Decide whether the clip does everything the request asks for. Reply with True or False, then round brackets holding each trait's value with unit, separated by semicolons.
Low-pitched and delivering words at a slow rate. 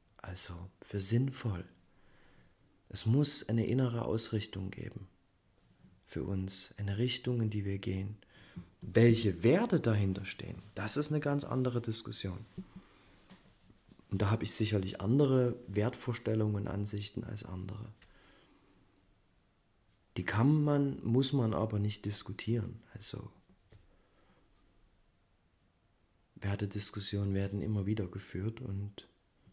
True (105 Hz; 110 wpm)